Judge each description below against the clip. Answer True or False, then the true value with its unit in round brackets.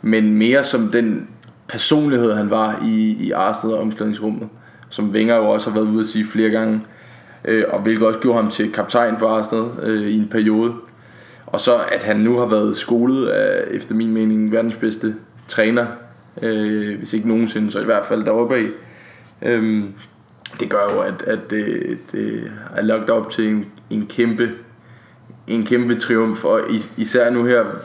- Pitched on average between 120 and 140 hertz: False (110 Hz)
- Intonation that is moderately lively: False (1.6 semitones)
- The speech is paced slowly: False (175 wpm)